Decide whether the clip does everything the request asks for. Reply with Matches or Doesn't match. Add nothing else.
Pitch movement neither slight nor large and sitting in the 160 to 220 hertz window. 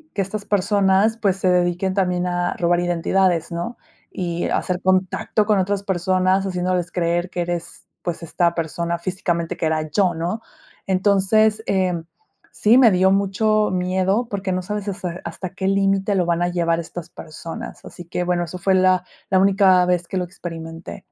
Doesn't match